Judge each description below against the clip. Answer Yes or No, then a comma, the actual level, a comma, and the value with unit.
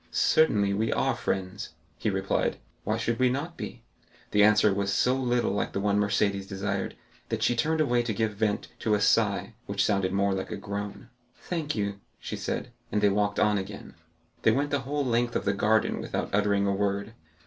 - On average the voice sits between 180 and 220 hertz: No, low, 105 Hz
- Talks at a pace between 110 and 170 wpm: No, average, 200 wpm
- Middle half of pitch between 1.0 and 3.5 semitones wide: Yes, average, 3.1 semitones